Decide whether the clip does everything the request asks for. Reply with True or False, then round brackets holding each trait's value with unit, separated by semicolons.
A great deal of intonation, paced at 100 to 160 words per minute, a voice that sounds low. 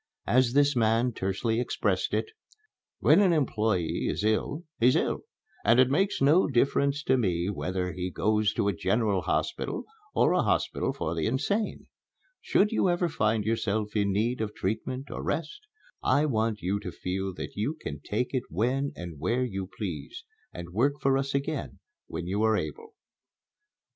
False (5.7 semitones; 170 wpm; 115 Hz)